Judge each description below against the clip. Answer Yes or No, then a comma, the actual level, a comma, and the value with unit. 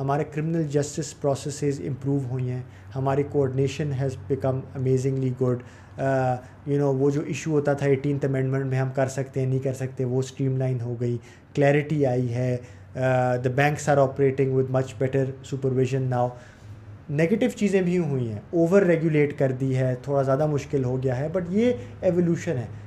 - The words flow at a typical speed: Yes, average, 175 wpm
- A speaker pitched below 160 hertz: Yes, low, 135 Hz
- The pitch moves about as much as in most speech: No, narrow, 2.0 semitones